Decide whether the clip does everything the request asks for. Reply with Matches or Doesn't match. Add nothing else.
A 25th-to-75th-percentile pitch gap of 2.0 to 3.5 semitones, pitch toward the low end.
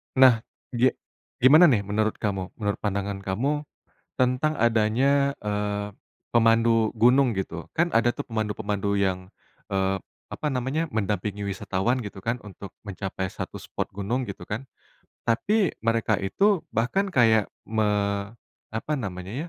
Doesn't match